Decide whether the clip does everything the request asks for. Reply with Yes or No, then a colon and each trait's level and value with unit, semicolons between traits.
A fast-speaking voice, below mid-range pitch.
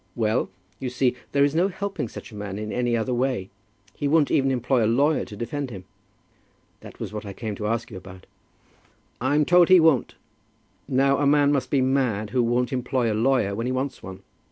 Yes: fast, 210 wpm; low, 125 Hz